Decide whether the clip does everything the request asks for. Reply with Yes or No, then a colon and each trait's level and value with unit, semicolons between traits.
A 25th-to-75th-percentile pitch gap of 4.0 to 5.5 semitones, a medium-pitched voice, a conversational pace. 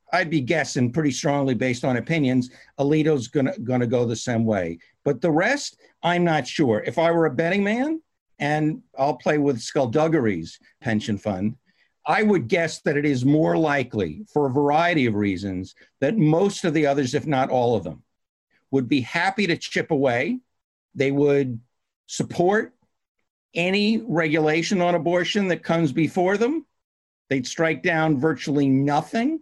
Yes: average, 4.6 semitones; medium, 150 Hz; average, 160 wpm